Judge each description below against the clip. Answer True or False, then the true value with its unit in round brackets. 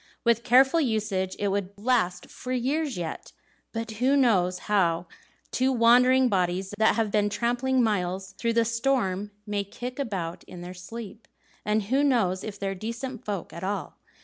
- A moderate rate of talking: True (165 wpm)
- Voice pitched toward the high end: True (215 Hz)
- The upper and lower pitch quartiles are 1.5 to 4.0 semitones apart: False (4.5 semitones)